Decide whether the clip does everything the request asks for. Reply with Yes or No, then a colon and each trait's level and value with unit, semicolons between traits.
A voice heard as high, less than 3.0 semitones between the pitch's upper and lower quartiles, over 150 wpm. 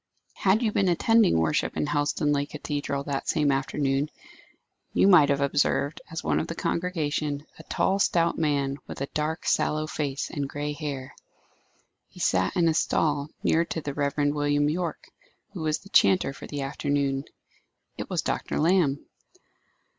No: medium, 145 Hz; narrow, 2.5 semitones; average, 160 wpm